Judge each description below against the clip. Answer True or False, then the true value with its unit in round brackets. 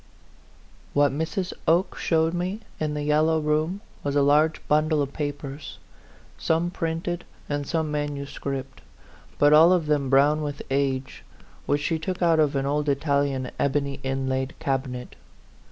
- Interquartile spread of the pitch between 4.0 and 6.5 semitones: False (2.4 semitones)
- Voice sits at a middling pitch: True (150 Hz)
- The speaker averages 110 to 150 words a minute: True (145 wpm)